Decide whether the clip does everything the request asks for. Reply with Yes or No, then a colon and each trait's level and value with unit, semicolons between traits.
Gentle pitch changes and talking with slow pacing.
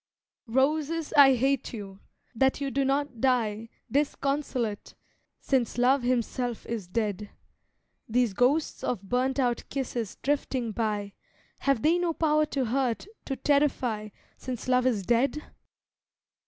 No: average, 3.4 semitones; slow, 125 wpm